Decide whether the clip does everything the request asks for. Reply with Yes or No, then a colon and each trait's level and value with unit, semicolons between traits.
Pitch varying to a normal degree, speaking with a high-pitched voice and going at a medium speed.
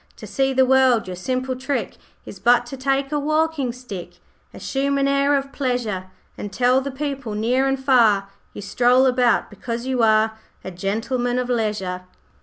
Yes: average, 3.6 semitones; very high, 250 Hz; average, 175 wpm